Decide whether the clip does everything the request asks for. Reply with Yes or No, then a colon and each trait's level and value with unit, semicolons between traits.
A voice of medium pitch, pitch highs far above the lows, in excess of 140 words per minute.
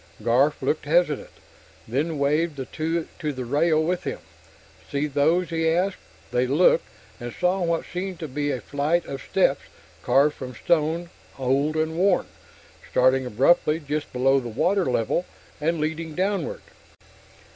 No: medium, 155 Hz; average, 3.8 semitones; average, 150 wpm